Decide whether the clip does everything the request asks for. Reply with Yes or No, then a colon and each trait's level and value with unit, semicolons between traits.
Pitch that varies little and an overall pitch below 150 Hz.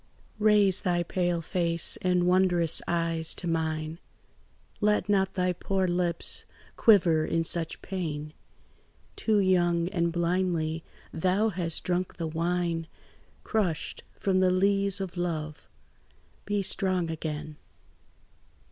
No: narrow, 2.3 semitones; medium, 175 Hz